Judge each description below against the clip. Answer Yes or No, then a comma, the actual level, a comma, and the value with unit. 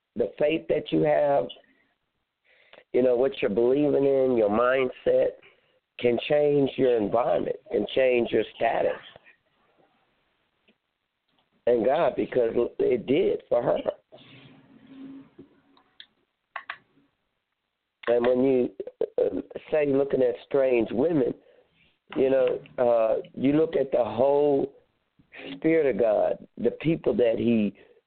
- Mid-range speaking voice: Yes, medium, 145 Hz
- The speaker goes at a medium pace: No, slow, 110 wpm